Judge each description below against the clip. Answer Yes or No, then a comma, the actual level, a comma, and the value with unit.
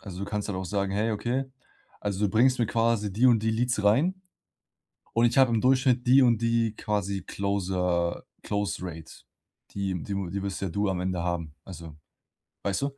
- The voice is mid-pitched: No, low, 105 Hz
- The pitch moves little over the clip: No, average, 3.8 semitones